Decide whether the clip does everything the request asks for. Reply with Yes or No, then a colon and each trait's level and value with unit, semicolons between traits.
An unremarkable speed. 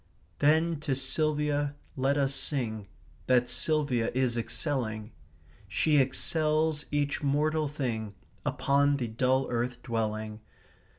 No: slow, 115 wpm